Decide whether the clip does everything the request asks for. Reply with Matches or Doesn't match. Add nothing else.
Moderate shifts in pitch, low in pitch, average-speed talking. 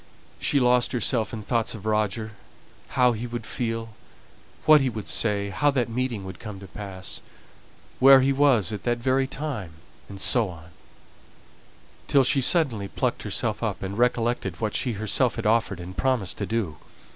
Matches